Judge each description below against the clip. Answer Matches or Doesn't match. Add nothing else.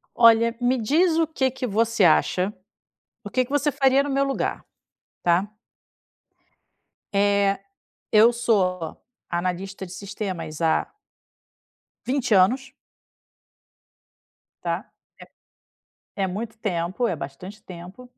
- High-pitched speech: Matches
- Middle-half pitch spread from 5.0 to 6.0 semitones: Matches